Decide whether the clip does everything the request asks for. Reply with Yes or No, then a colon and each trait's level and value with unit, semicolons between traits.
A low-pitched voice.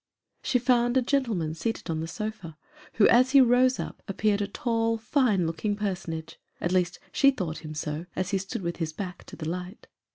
No: high, 200 Hz